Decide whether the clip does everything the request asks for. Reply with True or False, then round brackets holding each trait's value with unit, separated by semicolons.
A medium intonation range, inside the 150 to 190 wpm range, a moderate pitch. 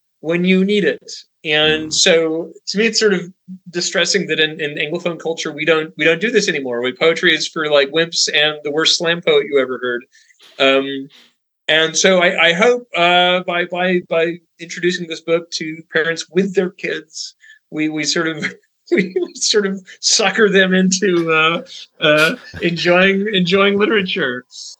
True (3.4 semitones; 170 wpm; 170 Hz)